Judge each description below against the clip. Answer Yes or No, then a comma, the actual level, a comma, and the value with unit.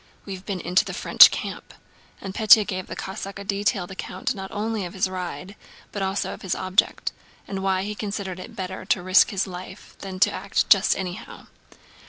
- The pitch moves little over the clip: Yes, narrow, 1.3 semitones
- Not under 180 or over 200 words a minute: Yes, average, 195 wpm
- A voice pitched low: No, high, 190 Hz